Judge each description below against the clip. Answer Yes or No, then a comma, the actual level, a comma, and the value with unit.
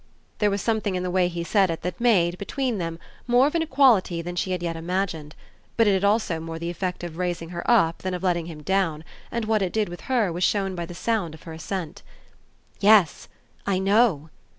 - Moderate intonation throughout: Yes, average, 3.7 semitones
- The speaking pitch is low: No, medium, 185 Hz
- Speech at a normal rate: No, fast, 225 wpm